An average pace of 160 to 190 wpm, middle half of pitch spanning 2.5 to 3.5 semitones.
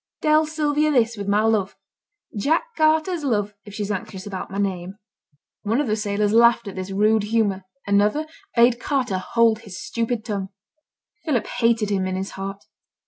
Yes: average, 170 wpm; average, 3.2 semitones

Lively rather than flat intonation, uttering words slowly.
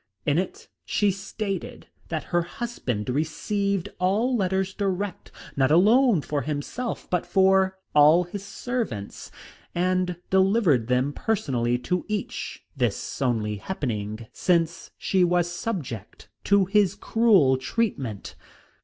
Yes: wide, 6.3 semitones; slow, 120 wpm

